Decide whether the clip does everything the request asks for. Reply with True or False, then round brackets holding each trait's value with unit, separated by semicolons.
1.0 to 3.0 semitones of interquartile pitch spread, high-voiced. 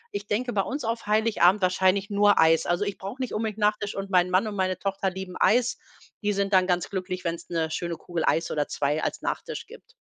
True (2.7 semitones; 195 Hz)